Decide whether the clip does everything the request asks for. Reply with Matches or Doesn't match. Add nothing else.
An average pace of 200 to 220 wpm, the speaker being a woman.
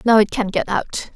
Doesn't match